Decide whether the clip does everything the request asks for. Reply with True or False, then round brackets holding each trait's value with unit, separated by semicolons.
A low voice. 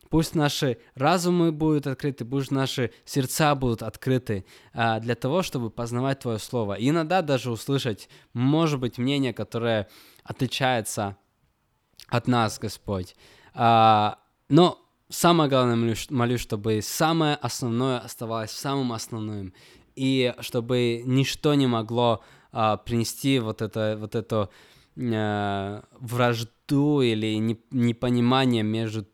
True (120 Hz)